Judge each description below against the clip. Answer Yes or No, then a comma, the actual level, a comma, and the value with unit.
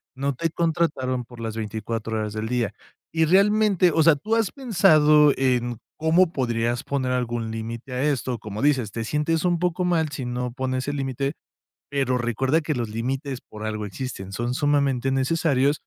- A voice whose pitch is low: Yes, low, 130 Hz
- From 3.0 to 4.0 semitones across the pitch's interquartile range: No, average, 4.7 semitones